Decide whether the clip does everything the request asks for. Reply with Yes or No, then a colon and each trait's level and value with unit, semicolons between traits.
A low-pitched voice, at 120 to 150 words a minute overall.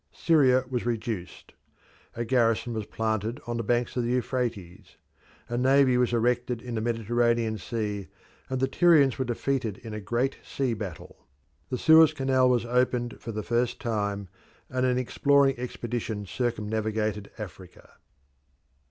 Yes: low, 120 Hz; average, 145 wpm